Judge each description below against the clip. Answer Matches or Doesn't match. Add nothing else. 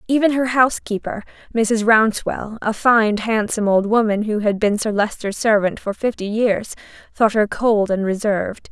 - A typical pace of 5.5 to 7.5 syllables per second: Doesn't match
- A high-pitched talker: Matches